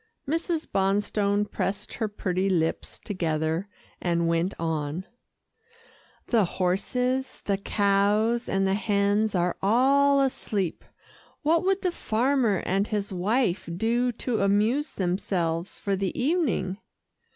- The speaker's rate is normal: No, slow, 120 wpm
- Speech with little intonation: No, average, 4.5 semitones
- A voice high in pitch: Yes, high, 200 Hz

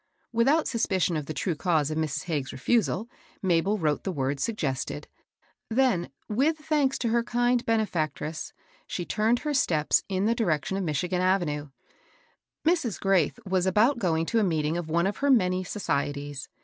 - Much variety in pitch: Yes, wide, 6.9 semitones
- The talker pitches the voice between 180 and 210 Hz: Yes, medium, 185 Hz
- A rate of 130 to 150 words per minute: No, average, 175 wpm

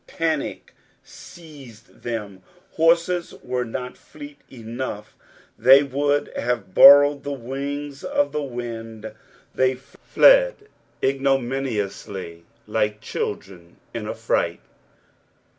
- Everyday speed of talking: No, slow, 95 wpm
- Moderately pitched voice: No, low, 130 Hz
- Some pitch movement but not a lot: Yes, average, 4.3 semitones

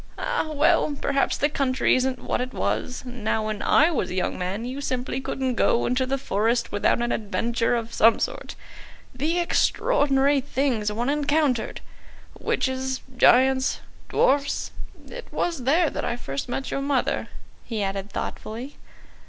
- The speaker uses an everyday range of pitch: Yes, average, 3.2 semitones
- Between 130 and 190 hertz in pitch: No, very high, 255 Hz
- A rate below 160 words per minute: Yes, average, 150 wpm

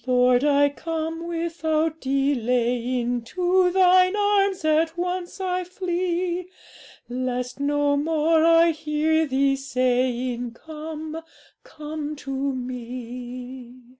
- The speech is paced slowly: Yes, slow, 100 wpm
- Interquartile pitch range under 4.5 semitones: No, average, 4.8 semitones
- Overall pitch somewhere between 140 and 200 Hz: No, very high, 300 Hz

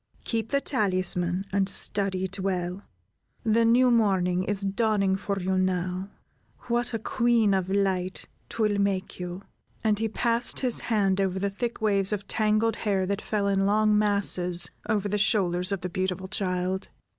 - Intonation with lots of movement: No, narrow, 2.4 semitones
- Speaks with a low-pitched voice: No, high, 200 Hz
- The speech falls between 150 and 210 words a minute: Yes, average, 165 wpm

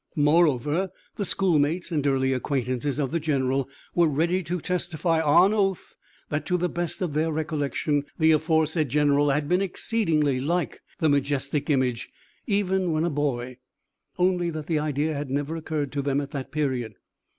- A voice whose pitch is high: No, medium, 150 Hz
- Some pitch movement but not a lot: Yes, average, 3.3 semitones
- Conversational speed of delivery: Yes, average, 165 wpm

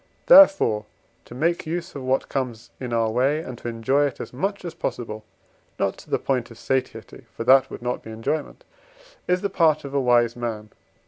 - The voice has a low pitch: Yes, low, 130 Hz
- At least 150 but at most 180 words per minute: No, average, 200 wpm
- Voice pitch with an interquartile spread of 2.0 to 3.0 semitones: No, average, 4.5 semitones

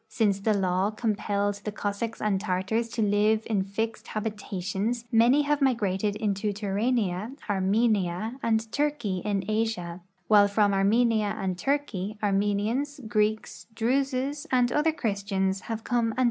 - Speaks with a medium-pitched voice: No, high, 215 Hz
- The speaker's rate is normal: No, slow, 130 wpm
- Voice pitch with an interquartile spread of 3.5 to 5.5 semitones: No, narrow, 2.6 semitones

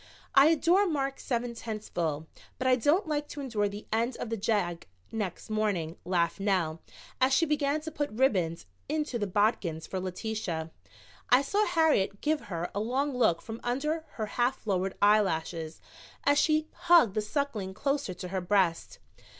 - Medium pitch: No, high, 220 Hz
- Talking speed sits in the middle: Yes, average, 170 wpm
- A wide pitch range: Yes, wide, 7.2 semitones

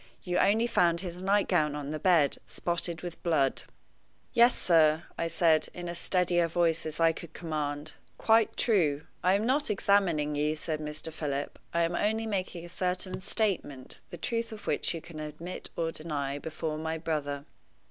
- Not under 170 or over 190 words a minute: Yes, average, 180 wpm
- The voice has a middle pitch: Yes, medium, 165 Hz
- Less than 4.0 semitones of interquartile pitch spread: Yes, average, 3.2 semitones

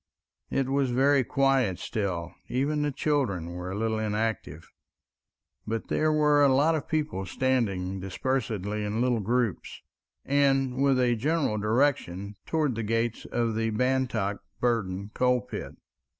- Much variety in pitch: No, average, 4.7 semitones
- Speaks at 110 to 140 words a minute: Yes, slow, 135 wpm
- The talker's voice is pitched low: Yes, low, 120 Hz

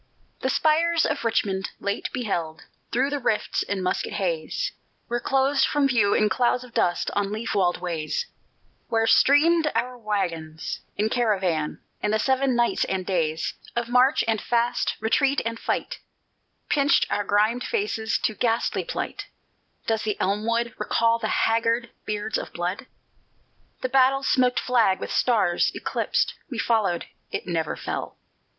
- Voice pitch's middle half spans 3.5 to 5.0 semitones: Yes, average, 4.3 semitones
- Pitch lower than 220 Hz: No, high, 230 Hz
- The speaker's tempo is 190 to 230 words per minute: No, average, 150 wpm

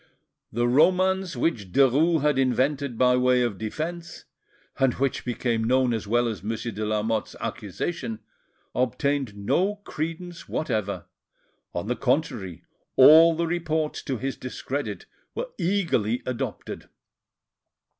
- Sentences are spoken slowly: Yes, slow, 125 wpm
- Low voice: Yes, low, 130 Hz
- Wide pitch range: Yes, wide, 5.8 semitones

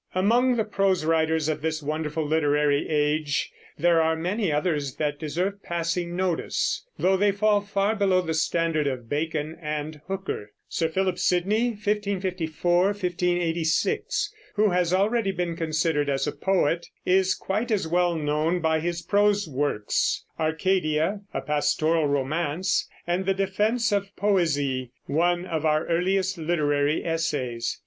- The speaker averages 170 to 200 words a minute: No, average, 140 wpm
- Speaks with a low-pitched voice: No, medium, 170 Hz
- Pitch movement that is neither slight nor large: Yes, average, 3.8 semitones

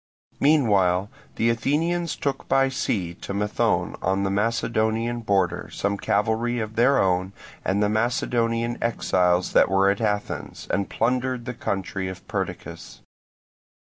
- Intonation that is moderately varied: Yes, average, 3.6 semitones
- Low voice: Yes, low, 110 Hz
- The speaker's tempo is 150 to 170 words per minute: No, slow, 135 wpm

